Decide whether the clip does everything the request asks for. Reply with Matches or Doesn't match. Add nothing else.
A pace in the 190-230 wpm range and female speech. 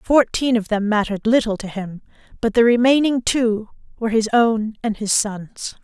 Doesn't match